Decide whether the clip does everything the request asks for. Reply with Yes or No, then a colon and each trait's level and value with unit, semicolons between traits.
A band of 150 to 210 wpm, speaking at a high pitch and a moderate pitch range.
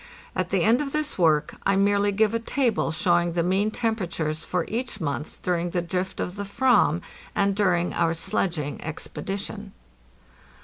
Yes: average, 170 wpm; high, 195 Hz; average, 3.6 semitones